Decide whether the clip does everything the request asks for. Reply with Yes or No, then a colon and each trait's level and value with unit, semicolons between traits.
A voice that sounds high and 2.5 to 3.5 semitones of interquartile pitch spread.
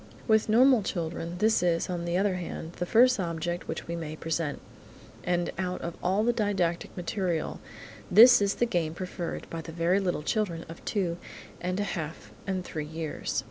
No: medium, 175 Hz; average, 3.2 semitones